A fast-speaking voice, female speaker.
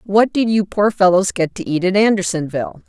Yes: fast, 210 wpm; female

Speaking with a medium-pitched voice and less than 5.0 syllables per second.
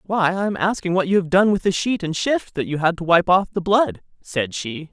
No: medium, 180 Hz; 5.2 syllables/s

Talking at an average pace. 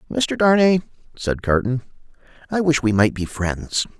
Yes: average, 150 wpm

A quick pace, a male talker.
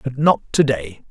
Yes: fast, 215 wpm; male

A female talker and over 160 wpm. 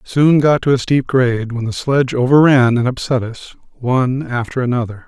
No: male; average, 190 wpm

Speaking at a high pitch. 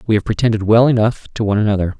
No: low, 110 Hz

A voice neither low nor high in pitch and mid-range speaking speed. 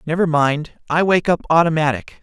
Yes: medium, 160 Hz; average, 160 wpm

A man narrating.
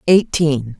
No: female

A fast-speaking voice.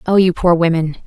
Yes: fast, 225 wpm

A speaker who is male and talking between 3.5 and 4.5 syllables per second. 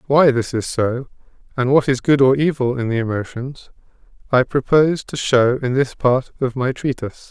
No: male; 5.0 syllables/s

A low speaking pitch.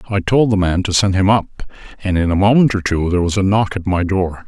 Yes: very low, 95 Hz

